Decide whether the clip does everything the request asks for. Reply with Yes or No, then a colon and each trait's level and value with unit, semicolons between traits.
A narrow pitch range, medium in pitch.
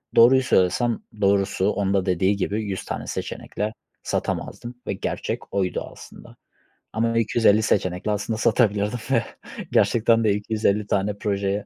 No: narrow, 2.3 semitones; low, 105 Hz